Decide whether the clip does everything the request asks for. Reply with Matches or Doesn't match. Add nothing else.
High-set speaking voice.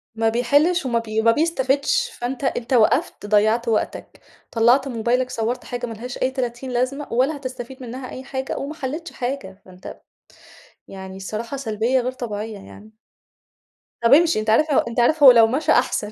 Matches